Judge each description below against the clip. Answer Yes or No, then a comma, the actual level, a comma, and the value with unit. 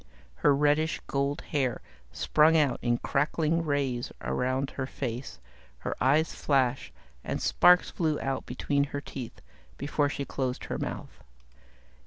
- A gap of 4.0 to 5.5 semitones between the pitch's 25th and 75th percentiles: No, narrow, 2.5 semitones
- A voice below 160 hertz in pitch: Yes, medium, 140 Hz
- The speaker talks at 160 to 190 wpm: No, slow, 135 wpm